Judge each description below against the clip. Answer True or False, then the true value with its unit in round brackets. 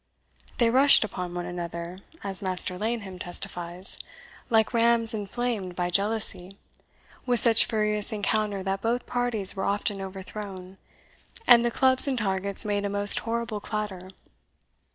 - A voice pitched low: False (205 Hz)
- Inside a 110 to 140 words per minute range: True (135 wpm)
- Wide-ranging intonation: False (3.5 semitones)